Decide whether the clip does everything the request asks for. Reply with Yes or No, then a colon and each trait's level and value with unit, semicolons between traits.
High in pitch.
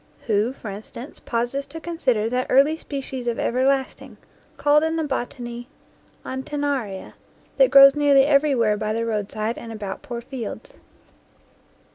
Yes: very high, 255 Hz